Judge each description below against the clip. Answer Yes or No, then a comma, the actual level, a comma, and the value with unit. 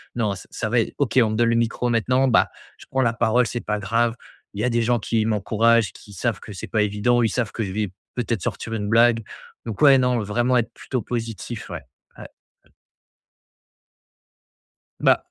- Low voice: Yes, low, 115 Hz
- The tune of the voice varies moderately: No, narrow, 2.1 semitones